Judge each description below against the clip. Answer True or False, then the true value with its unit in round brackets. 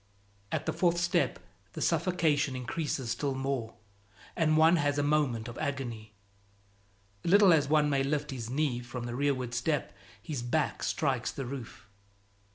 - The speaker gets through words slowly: False (155 wpm)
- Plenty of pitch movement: False (3.9 semitones)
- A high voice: False (140 Hz)